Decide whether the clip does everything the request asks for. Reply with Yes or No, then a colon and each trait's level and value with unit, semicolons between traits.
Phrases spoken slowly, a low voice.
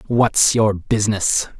Yes: slow, 115 wpm; low, 105 Hz